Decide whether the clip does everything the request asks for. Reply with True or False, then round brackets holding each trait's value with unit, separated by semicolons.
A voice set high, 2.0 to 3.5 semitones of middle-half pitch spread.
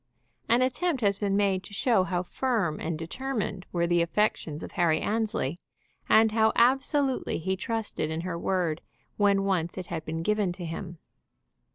False (195 Hz; 4.5 semitones)